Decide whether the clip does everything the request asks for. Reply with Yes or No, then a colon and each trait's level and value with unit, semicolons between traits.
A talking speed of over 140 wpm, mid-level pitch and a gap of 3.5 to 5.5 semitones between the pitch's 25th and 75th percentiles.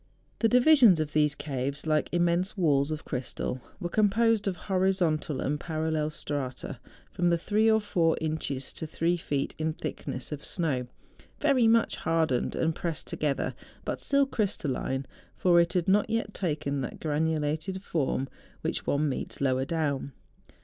Yes: average, 150 wpm; medium, 160 Hz; average, 4.6 semitones